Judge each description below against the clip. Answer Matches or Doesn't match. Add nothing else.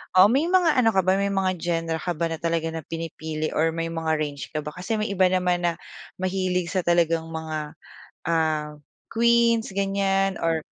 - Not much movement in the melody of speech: Doesn't match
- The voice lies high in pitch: Doesn't match